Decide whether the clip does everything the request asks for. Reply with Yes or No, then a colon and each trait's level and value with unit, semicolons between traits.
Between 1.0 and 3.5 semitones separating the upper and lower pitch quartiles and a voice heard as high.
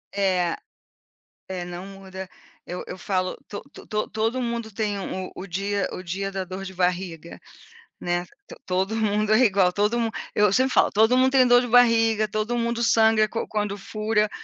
Yes: average, 3.0 semitones; high, 205 Hz